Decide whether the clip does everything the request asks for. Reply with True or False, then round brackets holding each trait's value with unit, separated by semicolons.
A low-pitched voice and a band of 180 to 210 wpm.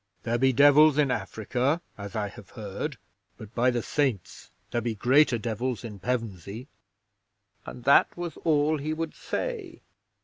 False (125 Hz; 150 wpm)